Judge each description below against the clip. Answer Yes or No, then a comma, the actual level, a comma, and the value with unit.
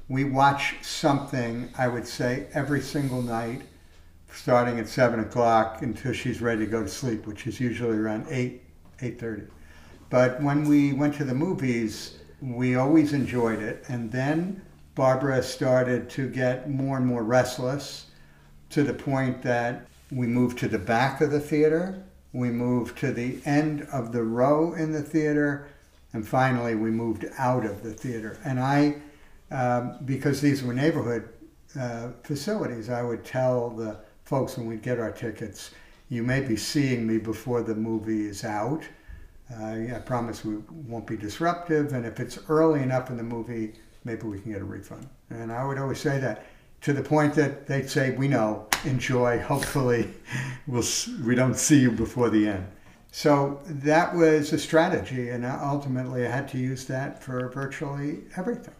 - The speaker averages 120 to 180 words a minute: Yes, average, 170 wpm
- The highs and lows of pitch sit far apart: No, average, 3.7 semitones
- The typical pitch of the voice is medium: No, low, 125 Hz